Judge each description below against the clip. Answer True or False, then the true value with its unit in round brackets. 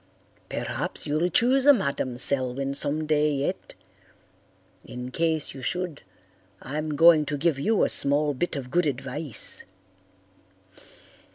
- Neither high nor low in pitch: True (150 Hz)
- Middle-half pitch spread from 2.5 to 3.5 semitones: True (3.1 semitones)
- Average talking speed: False (125 wpm)